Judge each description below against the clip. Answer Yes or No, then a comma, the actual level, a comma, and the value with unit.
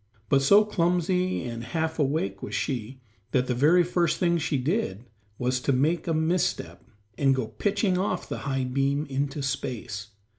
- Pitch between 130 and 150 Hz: Yes, medium, 140 Hz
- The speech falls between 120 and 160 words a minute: No, average, 170 wpm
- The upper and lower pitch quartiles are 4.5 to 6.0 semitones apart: Yes, average, 5.2 semitones